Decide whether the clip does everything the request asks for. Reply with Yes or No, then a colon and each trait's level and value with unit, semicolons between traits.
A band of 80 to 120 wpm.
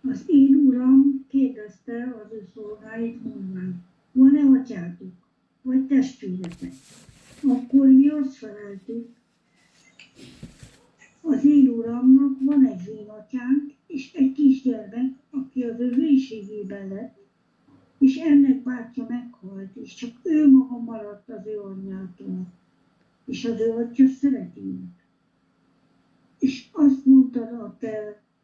Yes: average, 110 wpm